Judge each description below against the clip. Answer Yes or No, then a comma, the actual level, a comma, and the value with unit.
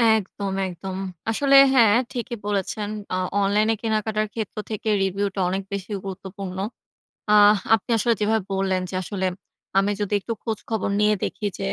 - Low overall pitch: No, high, 205 Hz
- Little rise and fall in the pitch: Yes, narrow, 2.2 semitones